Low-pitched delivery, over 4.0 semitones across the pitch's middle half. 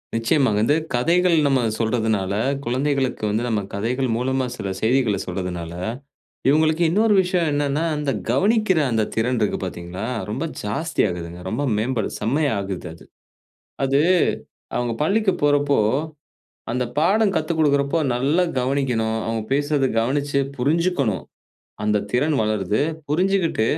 Yes: low, 130 Hz; wide, 5.6 semitones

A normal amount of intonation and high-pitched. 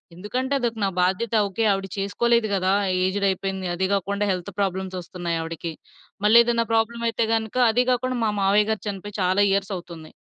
Yes: average, 3.2 semitones; high, 200 Hz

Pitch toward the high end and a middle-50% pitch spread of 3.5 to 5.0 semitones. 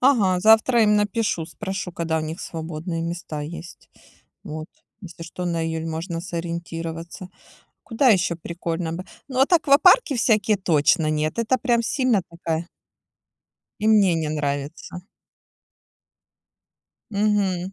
No: medium, 175 Hz; average, 4.5 semitones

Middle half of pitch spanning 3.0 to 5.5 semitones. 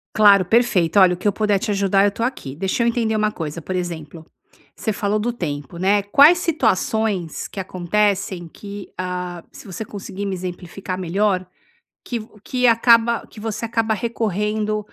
Yes: average, 3.3 semitones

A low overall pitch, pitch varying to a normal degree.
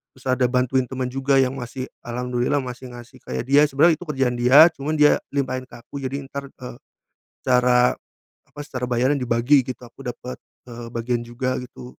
No: low, 125 Hz; narrow, 1.8 semitones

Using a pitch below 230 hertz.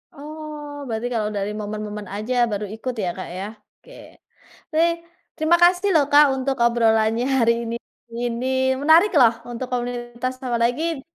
No: high, 245 Hz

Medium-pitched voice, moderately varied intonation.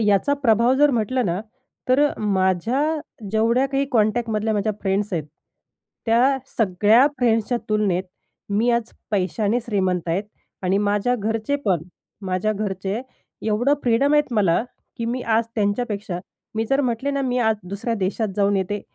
No: high, 220 Hz; average, 3.3 semitones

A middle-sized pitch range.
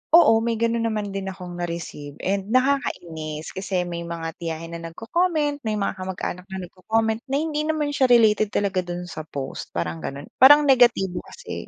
No: wide, 6.1 semitones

